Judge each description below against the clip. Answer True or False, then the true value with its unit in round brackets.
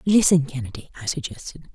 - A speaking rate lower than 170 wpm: True (140 wpm)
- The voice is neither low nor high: True (155 Hz)